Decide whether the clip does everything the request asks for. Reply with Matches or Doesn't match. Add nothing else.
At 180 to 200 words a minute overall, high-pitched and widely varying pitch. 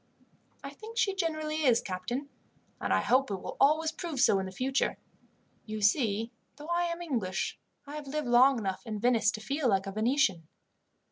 Matches